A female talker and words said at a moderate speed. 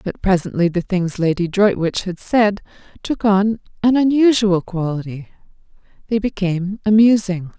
No: female; slow, 125 wpm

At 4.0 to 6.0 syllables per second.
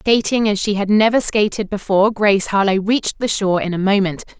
No: 6.2 syllables/s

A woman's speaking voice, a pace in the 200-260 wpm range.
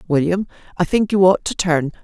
Yes: female; fast, 205 wpm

